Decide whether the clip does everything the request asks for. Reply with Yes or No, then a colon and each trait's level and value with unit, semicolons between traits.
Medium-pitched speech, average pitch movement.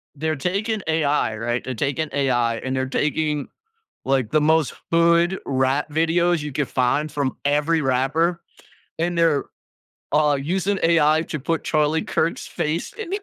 Yes: medium, 150 Hz; average, 3.5 semitones